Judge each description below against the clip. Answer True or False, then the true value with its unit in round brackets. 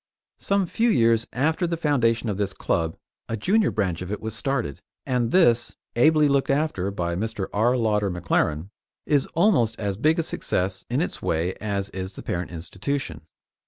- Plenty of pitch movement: True (6.9 semitones)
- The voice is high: False (115 Hz)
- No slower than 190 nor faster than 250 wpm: False (175 wpm)